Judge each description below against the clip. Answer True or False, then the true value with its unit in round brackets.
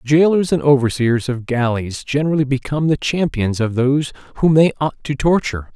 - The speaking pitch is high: False (135 Hz)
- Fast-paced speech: False (165 wpm)